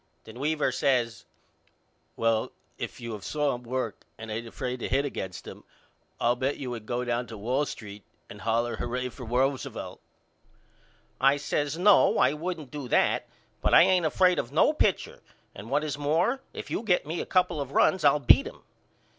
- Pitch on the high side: No, low, 135 Hz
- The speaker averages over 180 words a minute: Yes, average, 190 wpm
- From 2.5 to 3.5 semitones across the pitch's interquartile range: No, average, 4.3 semitones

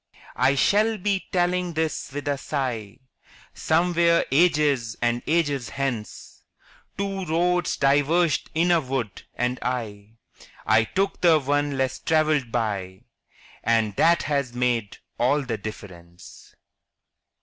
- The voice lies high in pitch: No, medium, 140 Hz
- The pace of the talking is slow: Yes, slow, 120 wpm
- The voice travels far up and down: Yes, wide, 6.1 semitones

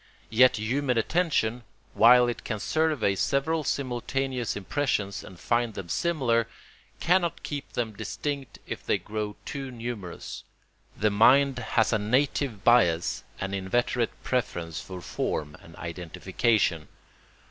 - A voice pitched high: No, low, 120 Hz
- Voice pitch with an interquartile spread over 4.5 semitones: Yes, average, 5.2 semitones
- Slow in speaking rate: Yes, slow, 125 wpm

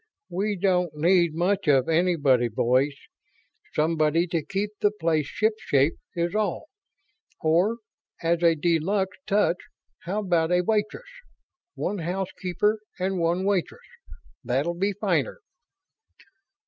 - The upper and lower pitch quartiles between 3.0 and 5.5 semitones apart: Yes, average, 3.7 semitones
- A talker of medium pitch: Yes, medium, 175 Hz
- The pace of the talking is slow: Yes, slow, 120 wpm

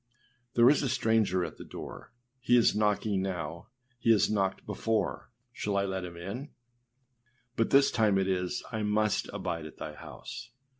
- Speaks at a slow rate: No, average, 170 wpm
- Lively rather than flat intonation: No, average, 3.7 semitones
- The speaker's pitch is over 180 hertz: No, low, 105 Hz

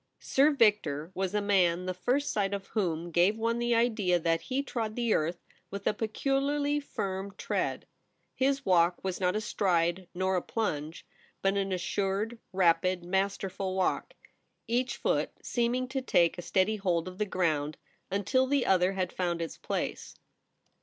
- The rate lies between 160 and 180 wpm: Yes, average, 165 wpm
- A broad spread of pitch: No, average, 4.3 semitones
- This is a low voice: No, high, 195 Hz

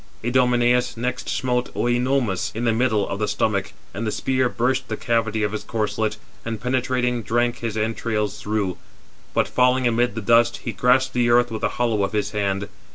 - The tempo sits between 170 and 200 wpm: Yes, average, 185 wpm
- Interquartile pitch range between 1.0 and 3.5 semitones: Yes, narrow, 2.4 semitones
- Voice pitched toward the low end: Yes, low, 115 Hz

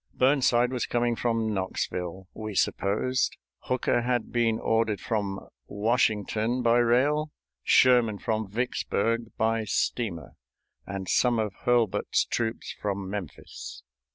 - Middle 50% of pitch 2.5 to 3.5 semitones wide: Yes, average, 3.0 semitones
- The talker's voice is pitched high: No, low, 115 Hz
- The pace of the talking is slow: Yes, slow, 115 wpm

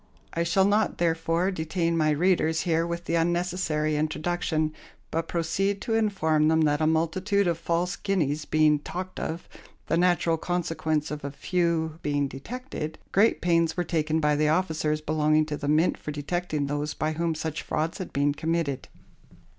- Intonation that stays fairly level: Yes, narrow, 2.3 semitones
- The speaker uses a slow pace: No, average, 170 wpm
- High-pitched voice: No, medium, 160 Hz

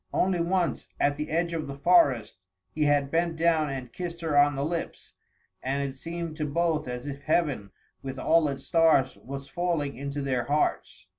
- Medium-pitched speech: Yes, medium, 145 Hz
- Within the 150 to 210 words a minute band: Yes, average, 190 wpm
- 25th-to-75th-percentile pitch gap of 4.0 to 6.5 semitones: No, average, 3.4 semitones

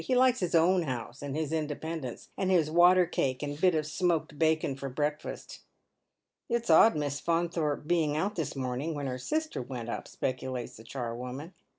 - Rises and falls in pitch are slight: No, average, 4.3 semitones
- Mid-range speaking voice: Yes, medium, 155 Hz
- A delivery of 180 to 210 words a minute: Yes, average, 185 wpm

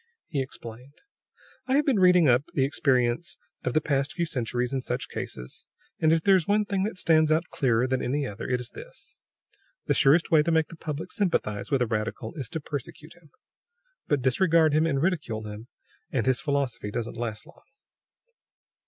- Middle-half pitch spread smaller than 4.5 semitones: No, average, 5.1 semitones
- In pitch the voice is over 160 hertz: No, medium, 140 Hz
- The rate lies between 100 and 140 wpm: No, average, 190 wpm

